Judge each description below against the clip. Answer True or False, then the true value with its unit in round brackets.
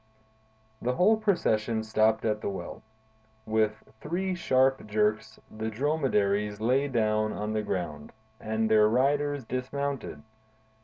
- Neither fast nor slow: False (120 wpm)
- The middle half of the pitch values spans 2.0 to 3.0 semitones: False (4.2 semitones)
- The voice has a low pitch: True (110 Hz)